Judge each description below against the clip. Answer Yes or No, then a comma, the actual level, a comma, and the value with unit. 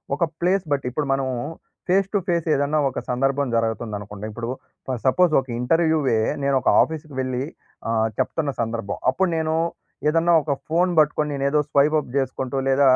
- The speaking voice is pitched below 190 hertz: Yes, medium, 140 Hz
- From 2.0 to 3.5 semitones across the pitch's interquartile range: No, average, 3.9 semitones